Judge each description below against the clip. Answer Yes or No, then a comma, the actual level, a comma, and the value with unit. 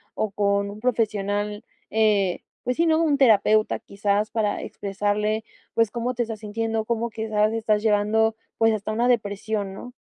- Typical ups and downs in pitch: No, narrow, 1.7 semitones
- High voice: Yes, high, 215 Hz